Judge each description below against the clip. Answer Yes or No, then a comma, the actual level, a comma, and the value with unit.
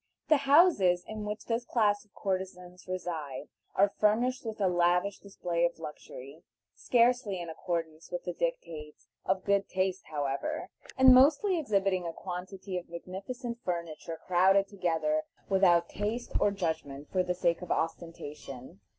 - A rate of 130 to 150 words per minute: Yes, average, 145 wpm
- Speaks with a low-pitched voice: No, medium, 185 Hz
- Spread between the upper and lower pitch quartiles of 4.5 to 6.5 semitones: No, average, 4.0 semitones